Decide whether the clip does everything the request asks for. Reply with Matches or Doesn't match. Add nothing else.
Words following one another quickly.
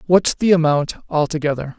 Doesn't match